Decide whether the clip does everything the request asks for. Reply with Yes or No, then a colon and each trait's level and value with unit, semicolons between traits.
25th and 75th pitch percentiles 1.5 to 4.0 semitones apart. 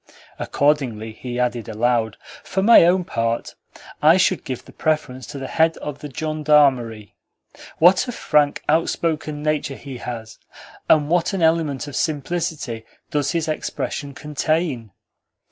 No: average, 4.5 semitones